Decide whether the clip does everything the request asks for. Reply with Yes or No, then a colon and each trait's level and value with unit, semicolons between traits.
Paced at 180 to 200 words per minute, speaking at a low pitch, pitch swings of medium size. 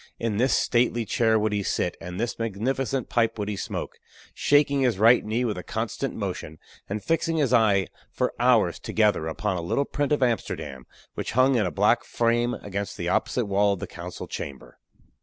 Yes: average, 195 wpm; low, 110 Hz; average, 3.9 semitones